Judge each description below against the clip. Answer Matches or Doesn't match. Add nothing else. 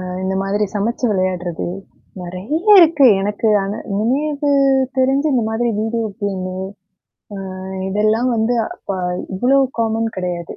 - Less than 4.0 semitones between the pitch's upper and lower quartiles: Doesn't match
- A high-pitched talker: Matches